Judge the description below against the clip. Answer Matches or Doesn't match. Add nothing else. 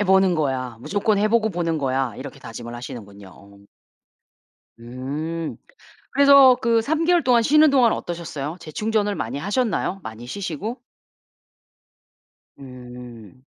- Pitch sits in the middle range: Matches